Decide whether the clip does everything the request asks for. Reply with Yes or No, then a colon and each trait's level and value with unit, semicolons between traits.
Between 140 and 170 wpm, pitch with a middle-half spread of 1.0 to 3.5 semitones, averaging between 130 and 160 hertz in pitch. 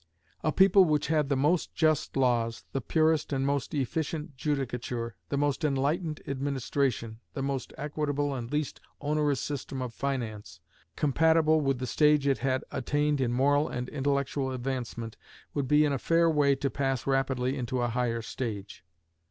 Yes: average, 160 wpm; average, 2.8 semitones; medium, 140 Hz